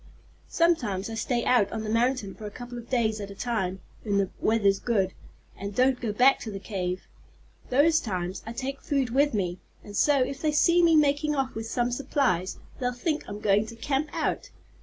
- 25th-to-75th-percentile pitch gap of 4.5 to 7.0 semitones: Yes, average, 5.1 semitones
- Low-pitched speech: No, high, 235 Hz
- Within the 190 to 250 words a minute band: Yes, fast, 205 wpm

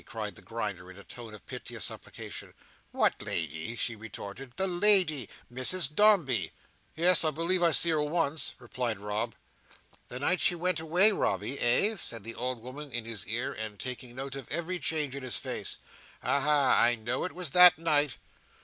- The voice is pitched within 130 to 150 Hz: Yes, low, 135 Hz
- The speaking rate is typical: Yes, average, 180 wpm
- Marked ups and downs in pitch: Yes, wide, 6.4 semitones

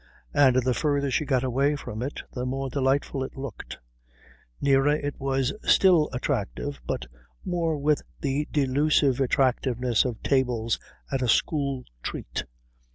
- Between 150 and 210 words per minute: No, average, 140 wpm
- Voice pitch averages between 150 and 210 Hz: No, low, 135 Hz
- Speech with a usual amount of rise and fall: No, narrow, 2.1 semitones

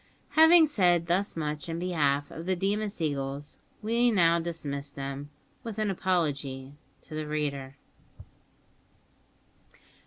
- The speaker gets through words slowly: Yes, slow, 120 wpm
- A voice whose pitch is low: No, medium, 165 Hz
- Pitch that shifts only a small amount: No, average, 5.2 semitones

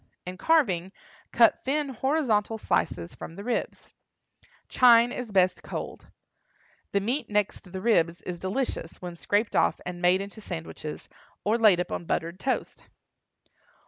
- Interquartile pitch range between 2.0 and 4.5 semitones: No, average, 5.0 semitones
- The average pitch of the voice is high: Yes, high, 200 Hz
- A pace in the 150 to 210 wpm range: No, average, 140 wpm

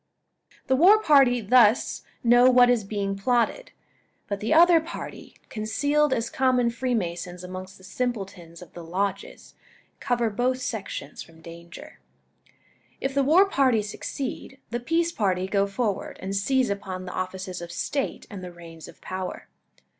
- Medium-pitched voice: No, high, 215 Hz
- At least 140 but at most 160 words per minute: Yes, average, 150 wpm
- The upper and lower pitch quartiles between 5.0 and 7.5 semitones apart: Yes, wide, 5.6 semitones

